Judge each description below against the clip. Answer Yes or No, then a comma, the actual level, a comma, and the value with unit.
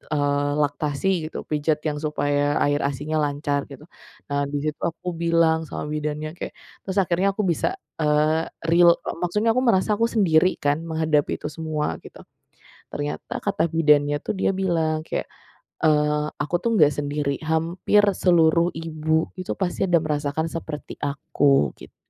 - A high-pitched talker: No, medium, 155 Hz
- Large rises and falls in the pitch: No, narrow, 2.6 semitones